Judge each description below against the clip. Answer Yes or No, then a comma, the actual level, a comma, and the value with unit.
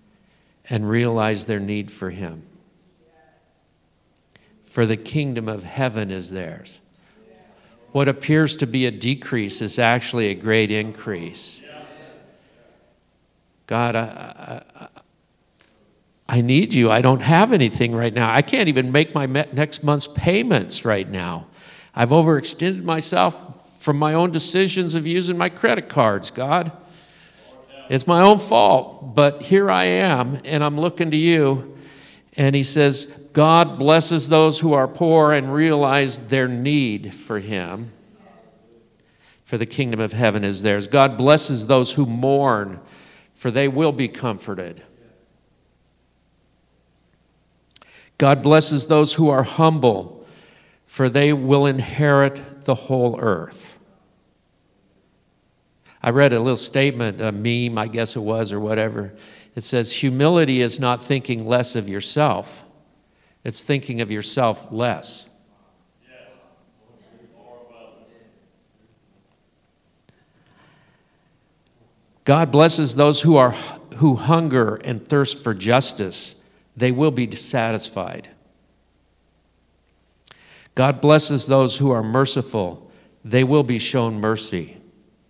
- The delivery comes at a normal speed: No, slow, 120 wpm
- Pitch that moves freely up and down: No, average, 5.0 semitones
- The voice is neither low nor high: No, low, 130 Hz